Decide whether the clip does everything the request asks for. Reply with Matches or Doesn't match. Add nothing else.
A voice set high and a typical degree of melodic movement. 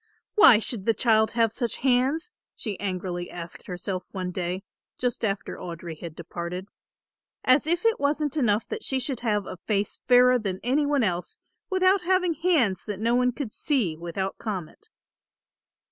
Doesn't match